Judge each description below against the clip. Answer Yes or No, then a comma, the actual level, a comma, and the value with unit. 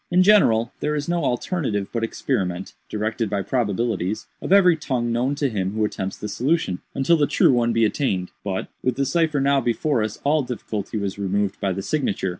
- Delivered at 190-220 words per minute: Yes, average, 200 wpm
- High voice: No, low, 120 Hz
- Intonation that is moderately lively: No, wide, 5.8 semitones